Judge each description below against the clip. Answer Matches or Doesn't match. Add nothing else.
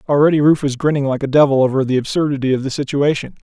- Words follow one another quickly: Matches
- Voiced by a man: Matches